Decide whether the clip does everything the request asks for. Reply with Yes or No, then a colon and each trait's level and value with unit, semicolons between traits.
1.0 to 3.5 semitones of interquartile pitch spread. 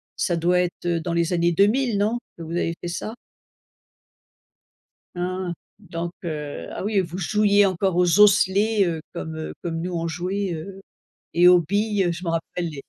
Yes: average, 2.9 semitones